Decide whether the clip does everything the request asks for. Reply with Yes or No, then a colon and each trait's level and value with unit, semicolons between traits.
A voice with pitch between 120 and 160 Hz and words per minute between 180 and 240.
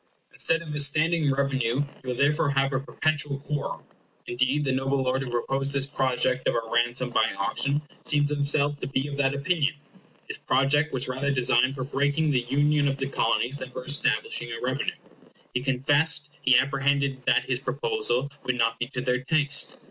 Yes: medium, 140 Hz; average, 185 wpm